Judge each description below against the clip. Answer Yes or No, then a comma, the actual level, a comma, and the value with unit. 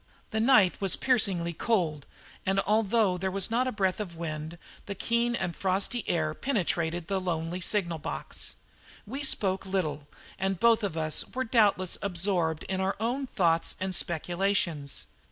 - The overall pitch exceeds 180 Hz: Yes, high, 190 Hz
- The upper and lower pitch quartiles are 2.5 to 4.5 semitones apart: Yes, average, 4.0 semitones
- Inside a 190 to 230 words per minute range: No, average, 160 wpm